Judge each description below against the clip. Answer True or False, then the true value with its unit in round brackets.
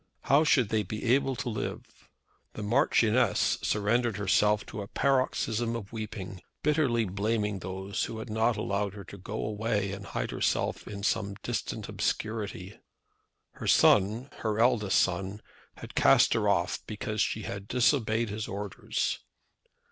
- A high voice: False (105 Hz)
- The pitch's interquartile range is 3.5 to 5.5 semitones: False (2.7 semitones)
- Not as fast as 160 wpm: True (150 wpm)